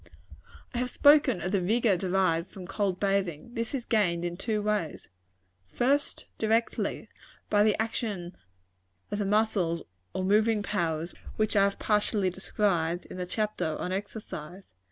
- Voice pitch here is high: Yes, high, 200 Hz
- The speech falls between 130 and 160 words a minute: Yes, average, 150 wpm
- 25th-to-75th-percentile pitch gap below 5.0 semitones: Yes, average, 3.5 semitones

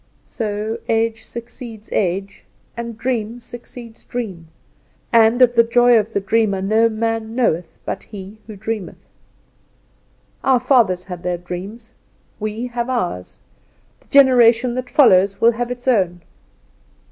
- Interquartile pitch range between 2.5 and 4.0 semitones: Yes, average, 3.3 semitones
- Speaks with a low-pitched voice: No, high, 225 Hz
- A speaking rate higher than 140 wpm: No, slow, 135 wpm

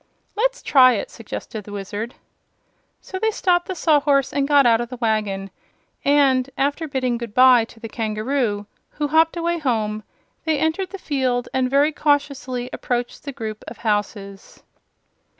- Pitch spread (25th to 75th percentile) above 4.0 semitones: Yes, average, 4.6 semitones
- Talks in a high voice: Yes, very high, 255 Hz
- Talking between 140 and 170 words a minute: Yes, average, 160 wpm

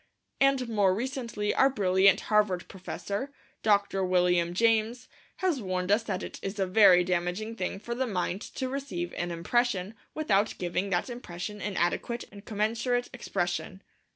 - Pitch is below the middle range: No, high, 205 Hz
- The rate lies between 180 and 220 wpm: No, average, 155 wpm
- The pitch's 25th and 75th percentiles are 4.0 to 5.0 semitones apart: Yes, average, 4.3 semitones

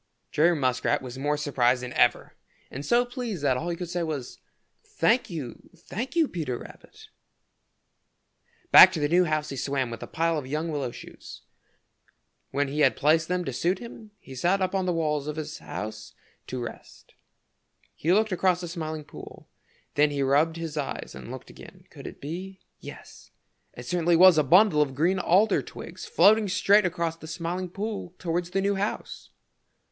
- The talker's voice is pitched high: No, medium, 165 Hz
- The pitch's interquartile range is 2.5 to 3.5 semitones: No, average, 4.5 semitones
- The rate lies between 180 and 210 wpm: Yes, average, 185 wpm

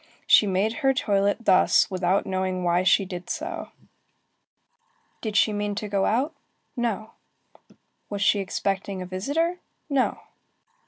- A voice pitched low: No, high, 205 Hz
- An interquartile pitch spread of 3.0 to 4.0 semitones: Yes, average, 3.6 semitones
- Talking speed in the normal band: No, slow, 130 wpm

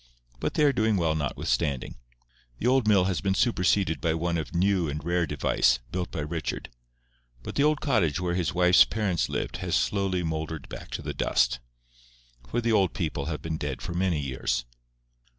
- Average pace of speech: Yes, average, 185 wpm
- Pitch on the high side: No, very low, 85 Hz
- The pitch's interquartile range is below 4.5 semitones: Yes, average, 4.1 semitones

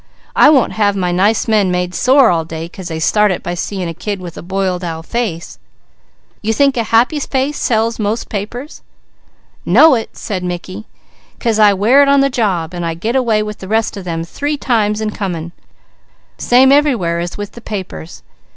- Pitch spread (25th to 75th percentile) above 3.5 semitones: Yes, average, 4.8 semitones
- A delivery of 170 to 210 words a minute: Yes, average, 195 wpm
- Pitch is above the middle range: Yes, high, 210 Hz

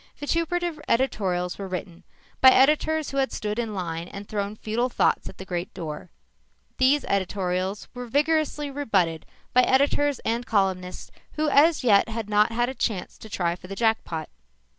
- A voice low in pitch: No, high, 220 Hz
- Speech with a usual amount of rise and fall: No, wide, 6.6 semitones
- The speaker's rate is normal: Yes, average, 165 wpm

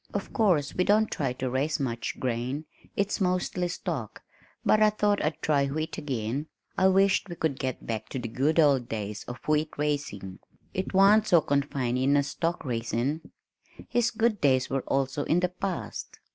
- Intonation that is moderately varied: No, wide, 6.0 semitones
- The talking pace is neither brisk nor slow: Yes, average, 175 wpm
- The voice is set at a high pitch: No, medium, 145 Hz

